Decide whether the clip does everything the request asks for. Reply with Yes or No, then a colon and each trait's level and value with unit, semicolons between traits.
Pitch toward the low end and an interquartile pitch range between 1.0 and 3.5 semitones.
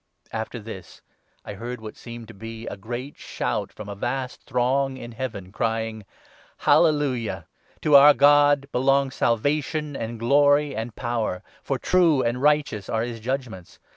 No: low, 120 Hz; average, 3.9 semitones